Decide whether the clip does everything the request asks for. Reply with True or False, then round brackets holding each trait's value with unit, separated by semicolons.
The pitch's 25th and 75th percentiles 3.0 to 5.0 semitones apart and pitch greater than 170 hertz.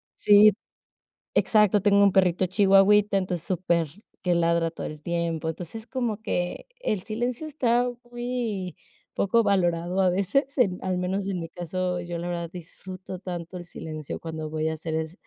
True (3.4 semitones; 185 Hz)